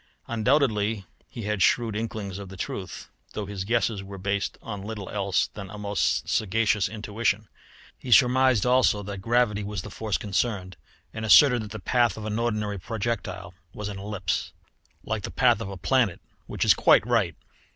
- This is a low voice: Yes, low, 105 Hz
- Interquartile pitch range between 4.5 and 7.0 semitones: No, narrow, 2.5 semitones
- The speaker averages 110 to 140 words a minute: No, average, 175 wpm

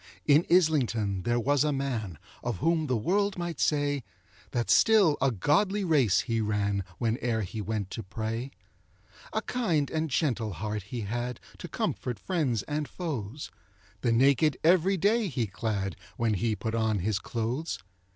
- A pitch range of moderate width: No, wide, 6.0 semitones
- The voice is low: Yes, low, 125 Hz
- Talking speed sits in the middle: Yes, average, 160 wpm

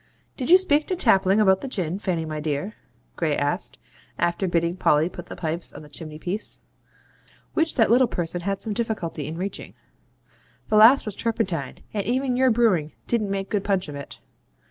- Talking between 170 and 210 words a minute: Yes, average, 190 wpm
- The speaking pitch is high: Yes, high, 195 Hz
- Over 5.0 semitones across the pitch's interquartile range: Yes, wide, 5.5 semitones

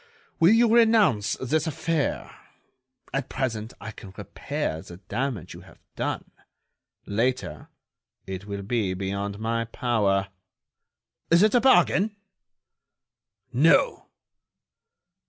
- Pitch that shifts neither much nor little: No, wide, 8.7 semitones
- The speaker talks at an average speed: No, slow, 105 wpm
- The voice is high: No, low, 120 Hz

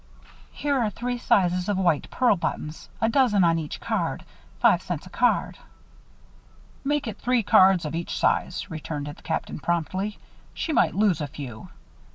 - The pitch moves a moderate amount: No, wide, 6.1 semitones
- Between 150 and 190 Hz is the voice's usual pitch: Yes, medium, 185 Hz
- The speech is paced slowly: No, average, 165 wpm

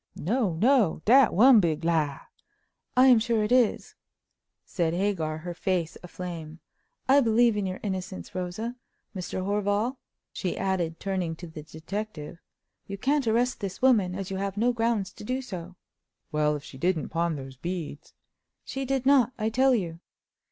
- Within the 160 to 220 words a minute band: Yes, average, 165 wpm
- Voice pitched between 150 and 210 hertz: Yes, high, 190 Hz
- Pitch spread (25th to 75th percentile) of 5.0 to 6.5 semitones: Yes, wide, 5.5 semitones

